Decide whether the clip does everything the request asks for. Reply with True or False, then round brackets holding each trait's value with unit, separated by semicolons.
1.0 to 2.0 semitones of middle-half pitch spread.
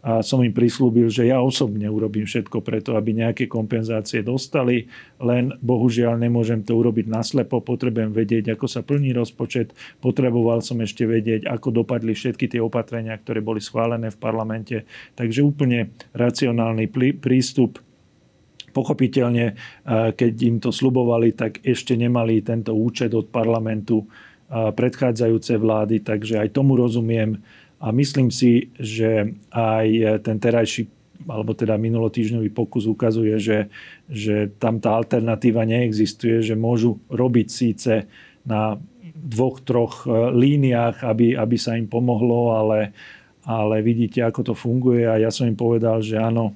True (1.7 semitones)